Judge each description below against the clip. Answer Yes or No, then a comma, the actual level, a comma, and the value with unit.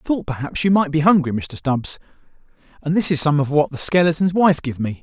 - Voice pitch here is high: No, medium, 155 Hz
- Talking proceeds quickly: Yes, fast, 240 wpm